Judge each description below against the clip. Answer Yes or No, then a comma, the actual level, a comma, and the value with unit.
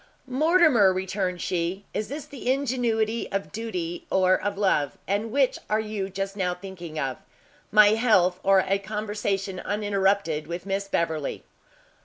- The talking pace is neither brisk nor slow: Yes, average, 145 wpm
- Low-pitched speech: No, high, 195 Hz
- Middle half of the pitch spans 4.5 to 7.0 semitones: No, average, 2.8 semitones